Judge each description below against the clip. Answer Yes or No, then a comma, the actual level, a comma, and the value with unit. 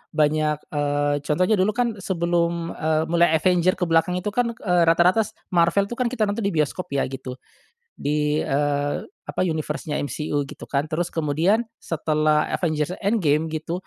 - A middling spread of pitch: Yes, average, 3.3 semitones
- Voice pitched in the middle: Yes, medium, 165 Hz